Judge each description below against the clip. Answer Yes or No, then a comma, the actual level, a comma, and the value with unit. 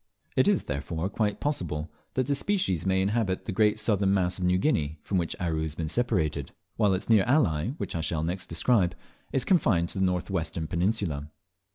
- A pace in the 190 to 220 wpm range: Yes, average, 200 wpm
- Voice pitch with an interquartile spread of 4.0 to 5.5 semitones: Yes, average, 4.8 semitones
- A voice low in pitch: Yes, very low, 95 Hz